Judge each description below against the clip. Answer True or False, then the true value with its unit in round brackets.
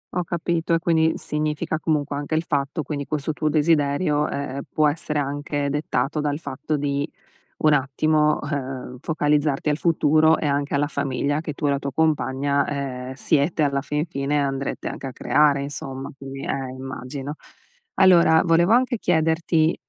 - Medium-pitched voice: True (145 Hz)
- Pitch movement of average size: False (2.2 semitones)